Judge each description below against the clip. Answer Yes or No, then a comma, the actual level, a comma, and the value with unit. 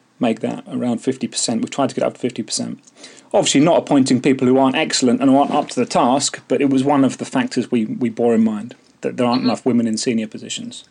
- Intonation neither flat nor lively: No, narrow, 2.2 semitones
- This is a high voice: No, low, 125 Hz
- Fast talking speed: Yes, fast, 250 wpm